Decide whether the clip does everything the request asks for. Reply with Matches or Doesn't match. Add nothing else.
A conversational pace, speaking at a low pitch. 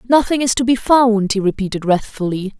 Doesn't match